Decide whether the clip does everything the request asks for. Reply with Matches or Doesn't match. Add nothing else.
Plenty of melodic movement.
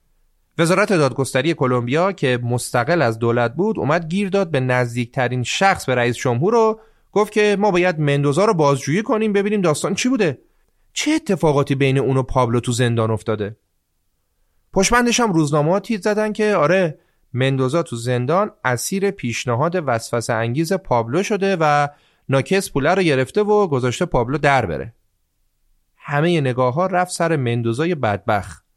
Matches